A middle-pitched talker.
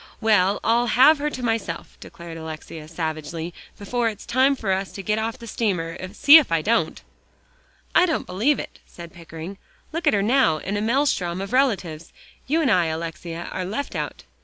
No: high, 200 Hz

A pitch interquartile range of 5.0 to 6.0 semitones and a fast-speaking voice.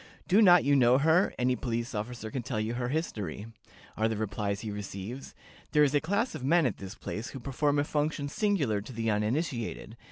Yes: average, 5.3 semitones; fast, 210 wpm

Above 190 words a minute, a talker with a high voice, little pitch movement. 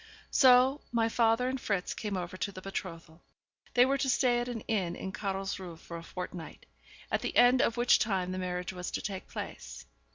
No: average, 200 wpm; high, 195 Hz; average, 5.0 semitones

